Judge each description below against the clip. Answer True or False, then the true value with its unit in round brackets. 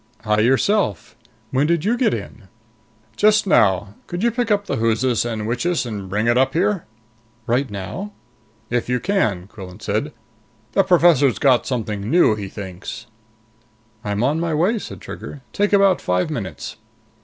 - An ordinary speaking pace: True (160 wpm)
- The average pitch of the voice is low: True (125 Hz)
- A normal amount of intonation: False (8.8 semitones)